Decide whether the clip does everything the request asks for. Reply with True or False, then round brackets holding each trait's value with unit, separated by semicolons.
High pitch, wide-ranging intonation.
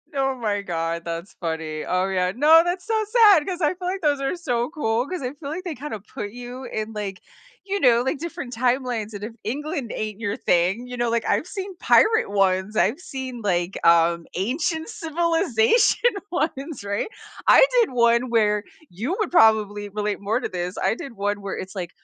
True (235 Hz; 7.4 semitones)